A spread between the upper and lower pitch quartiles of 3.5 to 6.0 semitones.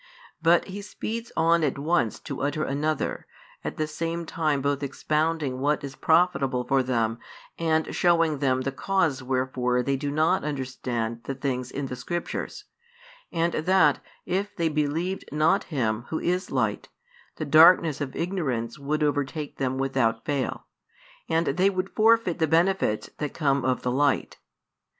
Yes: average, 4.0 semitones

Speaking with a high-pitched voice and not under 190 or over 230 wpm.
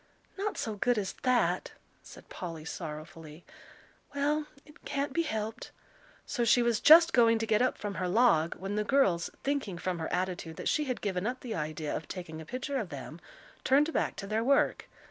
Yes: high, 220 Hz; average, 195 wpm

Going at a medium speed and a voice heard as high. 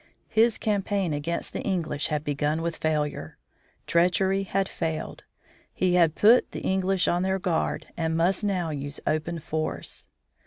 No: average, 150 wpm; medium, 170 Hz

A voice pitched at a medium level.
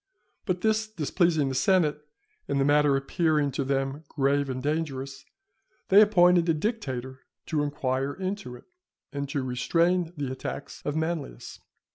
Yes: medium, 150 Hz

